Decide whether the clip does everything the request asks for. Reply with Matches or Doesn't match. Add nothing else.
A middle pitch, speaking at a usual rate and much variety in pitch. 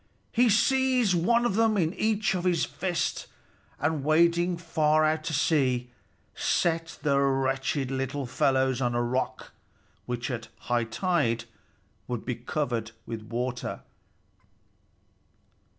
Doesn't match